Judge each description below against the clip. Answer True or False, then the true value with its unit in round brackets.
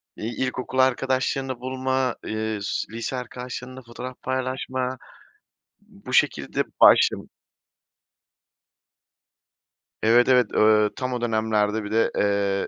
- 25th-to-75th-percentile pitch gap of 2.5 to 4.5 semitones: True (2.9 semitones)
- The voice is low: True (125 Hz)